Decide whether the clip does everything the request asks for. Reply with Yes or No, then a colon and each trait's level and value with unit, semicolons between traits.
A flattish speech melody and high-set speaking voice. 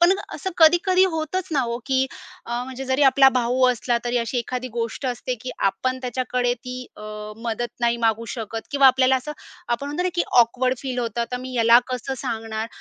Yes: narrow, 2.1 semitones; very high, 250 Hz